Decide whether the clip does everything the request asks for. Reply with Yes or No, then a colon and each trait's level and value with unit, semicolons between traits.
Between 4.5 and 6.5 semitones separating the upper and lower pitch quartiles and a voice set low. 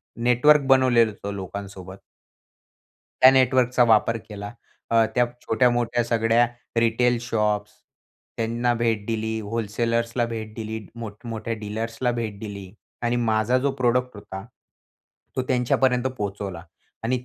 No: narrow, 2.4 semitones; low, 115 Hz